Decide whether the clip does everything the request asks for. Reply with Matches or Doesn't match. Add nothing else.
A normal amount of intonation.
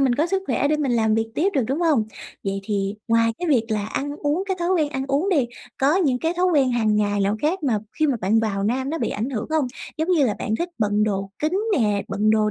Doesn't match